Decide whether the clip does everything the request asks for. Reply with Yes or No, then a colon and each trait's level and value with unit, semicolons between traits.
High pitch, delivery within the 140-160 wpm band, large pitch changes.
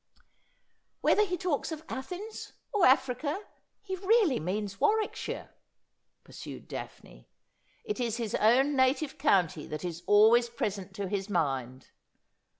Yes: very high, 250 Hz; average, 145 wpm; wide, 9.0 semitones